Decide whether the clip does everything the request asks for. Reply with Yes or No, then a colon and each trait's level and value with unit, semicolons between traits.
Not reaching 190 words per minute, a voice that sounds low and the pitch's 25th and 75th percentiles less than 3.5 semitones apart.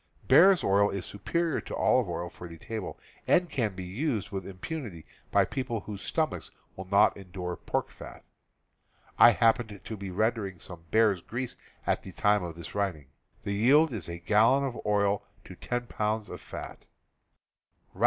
No: average, 170 wpm; low, 105 Hz; average, 4.2 semitones